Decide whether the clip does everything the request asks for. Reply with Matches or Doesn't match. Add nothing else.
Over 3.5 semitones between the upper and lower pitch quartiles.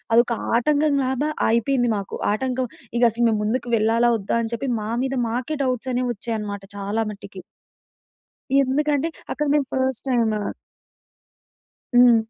Doesn't match